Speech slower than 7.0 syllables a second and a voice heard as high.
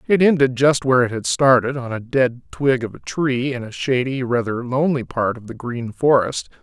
No: 5.1 syllables/s; low, 125 Hz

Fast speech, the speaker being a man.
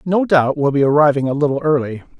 Yes: fast, 220 wpm; male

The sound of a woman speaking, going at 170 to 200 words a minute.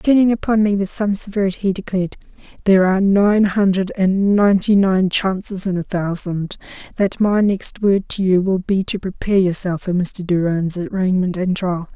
Yes: female; average, 180 wpm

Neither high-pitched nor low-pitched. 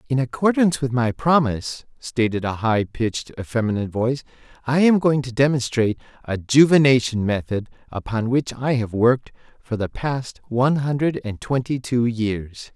No: low, 125 Hz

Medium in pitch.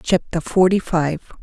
Yes: medium, 175 Hz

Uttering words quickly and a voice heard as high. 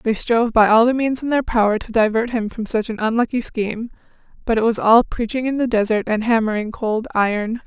Yes: fast, 225 wpm; high, 225 Hz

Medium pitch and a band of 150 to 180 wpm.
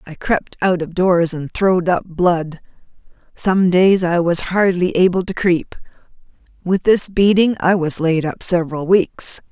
Yes: medium, 180 Hz; average, 165 wpm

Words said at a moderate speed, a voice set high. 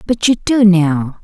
Yes: average, 195 wpm; high, 195 Hz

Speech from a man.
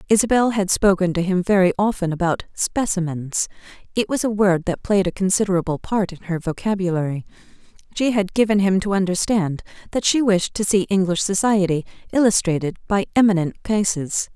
No: female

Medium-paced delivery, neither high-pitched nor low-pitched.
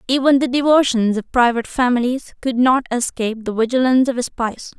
No: average, 175 wpm; high, 245 Hz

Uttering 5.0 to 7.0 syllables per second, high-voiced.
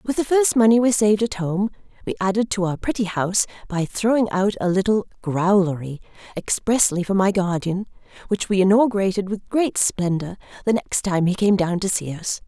Yes: 5.3 syllables/s; high, 200 Hz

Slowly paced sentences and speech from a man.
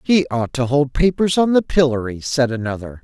No: average, 200 wpm; male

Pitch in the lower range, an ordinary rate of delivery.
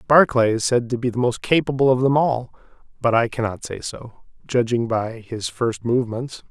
Yes: low, 120 Hz; average, 195 wpm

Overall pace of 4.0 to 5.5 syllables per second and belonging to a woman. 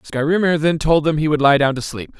No: 5.4 syllables/s; male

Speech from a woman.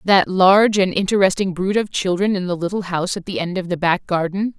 Yes: female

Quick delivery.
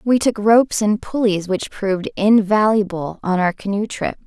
No: average, 170 wpm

